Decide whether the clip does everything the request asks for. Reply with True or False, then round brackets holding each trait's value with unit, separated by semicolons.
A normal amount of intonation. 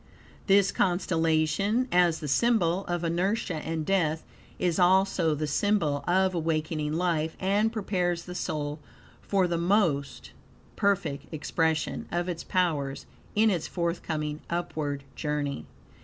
True (3.4 semitones)